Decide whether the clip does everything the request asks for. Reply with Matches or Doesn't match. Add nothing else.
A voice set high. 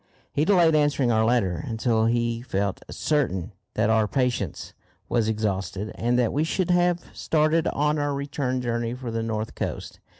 Doesn't match